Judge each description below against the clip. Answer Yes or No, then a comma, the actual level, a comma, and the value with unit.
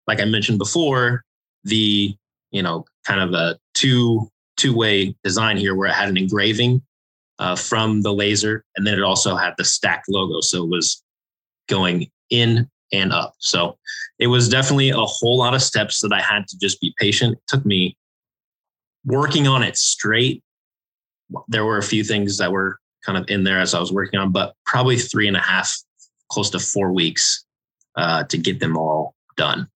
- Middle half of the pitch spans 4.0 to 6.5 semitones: No, average, 3.6 semitones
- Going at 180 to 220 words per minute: Yes, average, 190 wpm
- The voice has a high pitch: No, low, 105 Hz